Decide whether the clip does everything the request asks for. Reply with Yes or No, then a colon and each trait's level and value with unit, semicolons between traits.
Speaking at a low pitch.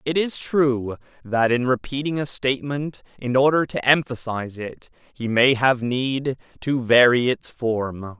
Yes: low, 130 Hz